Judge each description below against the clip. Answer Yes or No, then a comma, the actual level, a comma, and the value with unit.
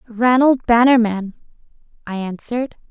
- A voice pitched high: Yes, high, 230 Hz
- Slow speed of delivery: Yes, slow, 85 wpm